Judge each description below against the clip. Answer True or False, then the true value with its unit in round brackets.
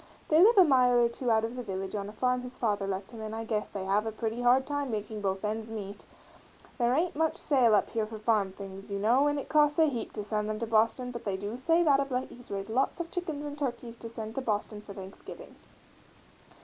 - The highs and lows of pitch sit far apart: False (3.9 semitones)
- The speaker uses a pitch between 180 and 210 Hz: False (230 Hz)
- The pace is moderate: False (250 wpm)